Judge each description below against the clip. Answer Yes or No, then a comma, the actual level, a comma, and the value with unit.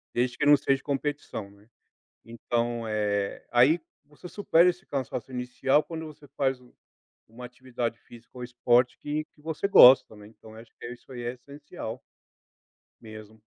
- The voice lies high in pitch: No, low, 125 Hz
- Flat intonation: No, average, 3.8 semitones